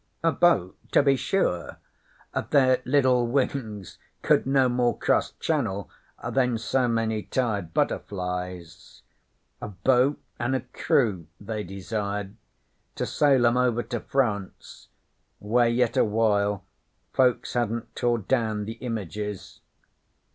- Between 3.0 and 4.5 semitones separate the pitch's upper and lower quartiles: Yes, average, 3.8 semitones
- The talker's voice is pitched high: No, low, 115 Hz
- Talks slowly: Yes, slow, 120 wpm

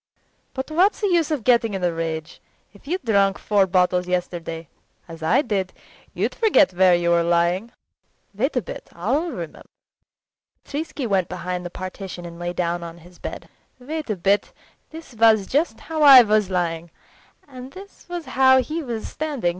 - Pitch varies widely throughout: Yes, wide, 7.4 semitones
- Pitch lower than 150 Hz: No, high, 200 Hz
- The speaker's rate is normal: Yes, average, 170 wpm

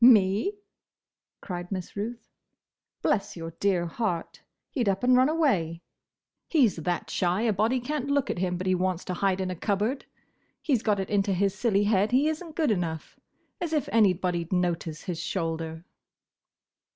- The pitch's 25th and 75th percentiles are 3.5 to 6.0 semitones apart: Yes, average, 5.1 semitones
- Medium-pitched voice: No, high, 195 Hz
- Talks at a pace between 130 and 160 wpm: No, average, 180 wpm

